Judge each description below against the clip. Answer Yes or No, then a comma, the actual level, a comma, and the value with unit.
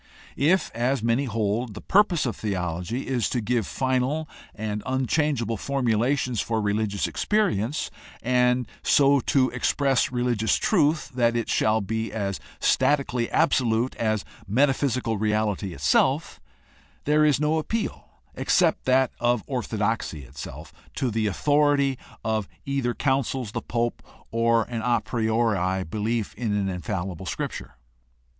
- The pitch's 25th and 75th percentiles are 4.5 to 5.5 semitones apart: No, average, 3.8 semitones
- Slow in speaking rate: Yes, slow, 130 wpm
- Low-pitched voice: Yes, low, 120 Hz